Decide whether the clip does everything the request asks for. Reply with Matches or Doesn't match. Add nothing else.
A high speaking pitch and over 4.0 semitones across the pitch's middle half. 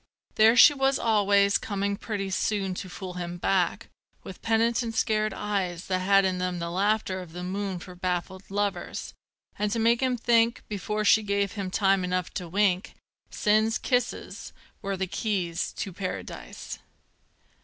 Doesn't match